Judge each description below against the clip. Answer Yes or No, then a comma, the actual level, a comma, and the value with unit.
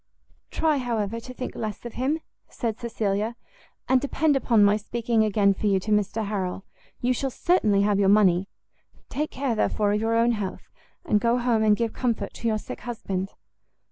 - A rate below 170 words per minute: No, average, 185 wpm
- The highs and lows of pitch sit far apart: No, average, 2.9 semitones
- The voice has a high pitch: Yes, high, 220 Hz